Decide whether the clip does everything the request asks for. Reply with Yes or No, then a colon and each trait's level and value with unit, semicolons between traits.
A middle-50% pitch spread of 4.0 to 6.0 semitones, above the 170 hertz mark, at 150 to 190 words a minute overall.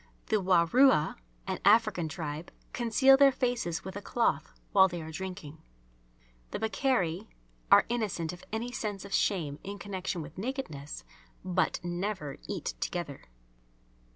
No: average, 4.8 semitones; high, 190 Hz; slow, 135 wpm